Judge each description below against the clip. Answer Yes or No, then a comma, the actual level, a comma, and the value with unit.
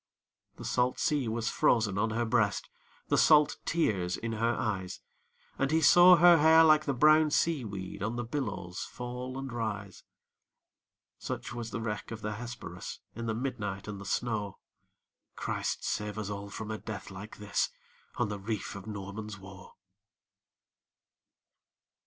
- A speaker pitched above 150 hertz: No, low, 110 Hz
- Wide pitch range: No, average, 3.7 semitones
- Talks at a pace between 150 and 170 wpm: Yes, average, 160 wpm